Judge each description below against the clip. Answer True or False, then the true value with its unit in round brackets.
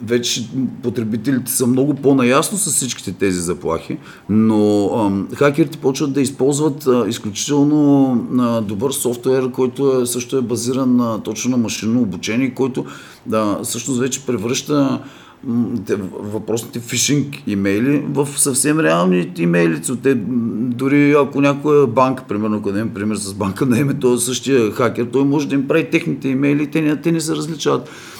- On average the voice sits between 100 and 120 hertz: False (130 Hz)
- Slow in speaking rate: False (155 wpm)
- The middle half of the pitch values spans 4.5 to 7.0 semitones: False (3.6 semitones)